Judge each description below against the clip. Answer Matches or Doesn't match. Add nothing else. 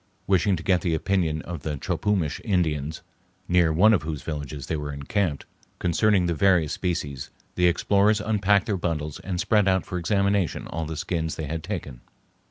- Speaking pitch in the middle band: Doesn't match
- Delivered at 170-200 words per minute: Matches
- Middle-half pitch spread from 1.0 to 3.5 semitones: Doesn't match